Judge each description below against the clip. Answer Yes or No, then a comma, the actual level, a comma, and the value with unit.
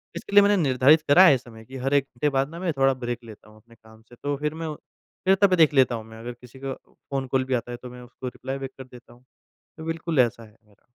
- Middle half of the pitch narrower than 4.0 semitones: Yes, average, 3.6 semitones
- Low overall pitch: Yes, low, 130 Hz